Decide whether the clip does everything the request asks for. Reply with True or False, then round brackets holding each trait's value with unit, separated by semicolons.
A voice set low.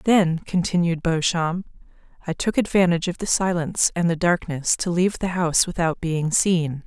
False (170 Hz)